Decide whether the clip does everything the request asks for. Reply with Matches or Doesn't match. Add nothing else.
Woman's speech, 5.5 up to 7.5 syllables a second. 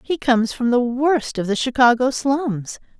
Doesn't match